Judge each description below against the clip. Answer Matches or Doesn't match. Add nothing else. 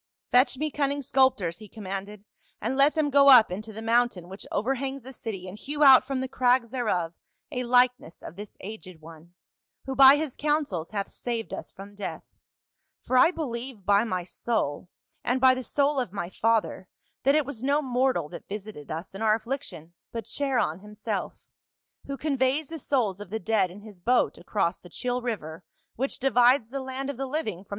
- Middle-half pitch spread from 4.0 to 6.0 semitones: Matches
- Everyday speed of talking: Doesn't match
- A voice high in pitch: Matches